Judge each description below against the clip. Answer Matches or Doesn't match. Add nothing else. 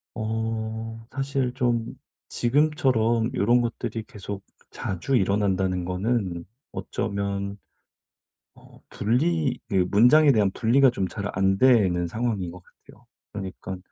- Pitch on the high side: Doesn't match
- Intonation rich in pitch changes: Doesn't match